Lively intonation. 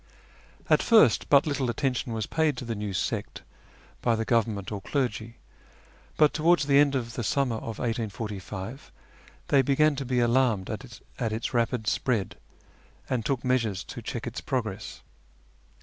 No: average, 3.6 semitones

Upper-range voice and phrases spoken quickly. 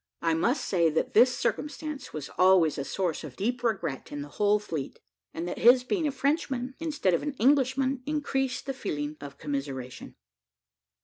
No: high, 210 Hz; average, 175 wpm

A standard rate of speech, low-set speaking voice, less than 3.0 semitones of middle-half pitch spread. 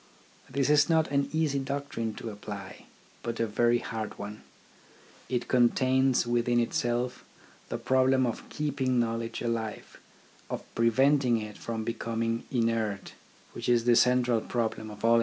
Yes: average, 145 wpm; low, 120 Hz; narrow, 2.4 semitones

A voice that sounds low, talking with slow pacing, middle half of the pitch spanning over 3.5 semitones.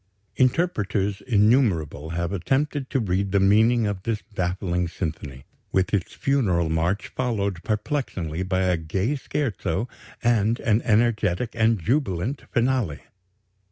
Yes: low, 100 Hz; slow, 120 wpm; average, 5.0 semitones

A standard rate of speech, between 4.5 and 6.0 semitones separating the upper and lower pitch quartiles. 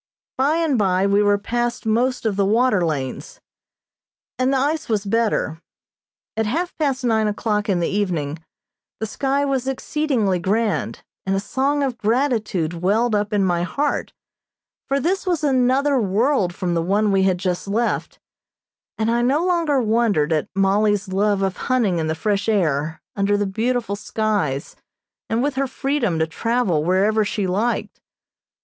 Yes: average, 165 wpm; average, 4.9 semitones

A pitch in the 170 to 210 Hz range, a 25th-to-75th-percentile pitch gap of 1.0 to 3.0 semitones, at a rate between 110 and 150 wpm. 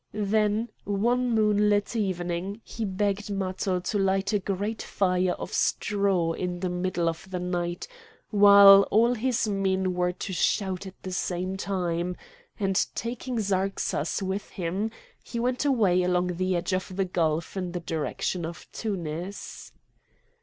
Yes: high, 190 Hz; narrow, 2.5 semitones; average, 145 wpm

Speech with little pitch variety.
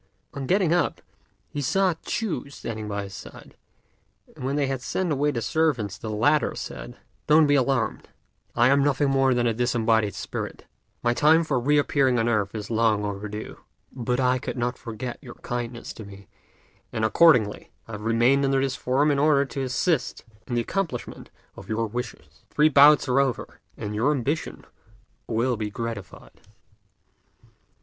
No: average, 4.1 semitones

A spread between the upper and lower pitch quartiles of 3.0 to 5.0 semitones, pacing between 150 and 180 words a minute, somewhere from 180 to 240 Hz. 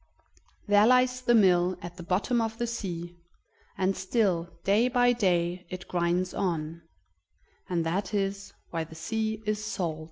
Yes: average, 4.1 semitones; average, 155 wpm; high, 190 Hz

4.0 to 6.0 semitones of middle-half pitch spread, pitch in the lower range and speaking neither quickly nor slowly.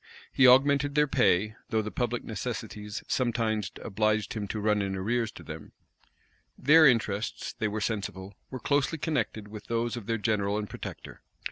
No: average, 3.2 semitones; low, 110 Hz; average, 165 wpm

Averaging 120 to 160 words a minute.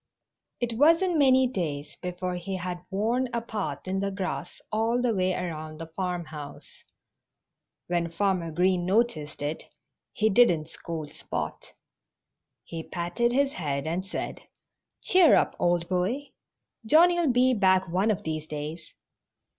Yes: average, 140 wpm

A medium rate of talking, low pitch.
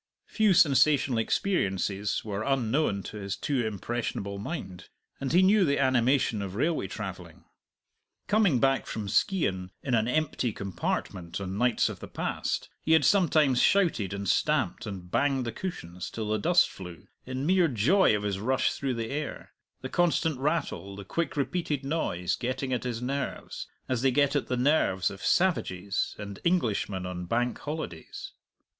Yes: average, 165 wpm; low, 125 Hz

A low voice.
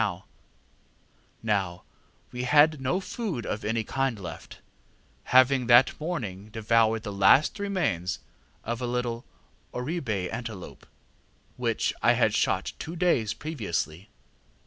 Yes: low, 120 Hz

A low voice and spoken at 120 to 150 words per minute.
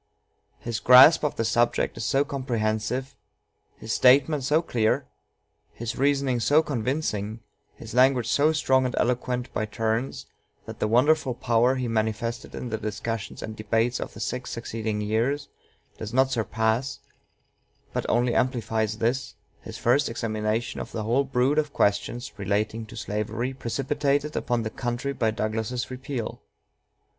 Yes: low, 120 Hz; average, 145 wpm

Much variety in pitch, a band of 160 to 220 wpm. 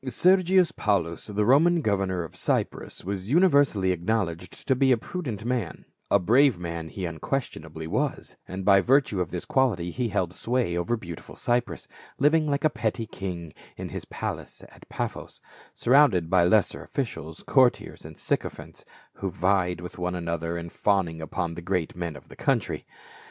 Yes: wide, 6.7 semitones; average, 165 wpm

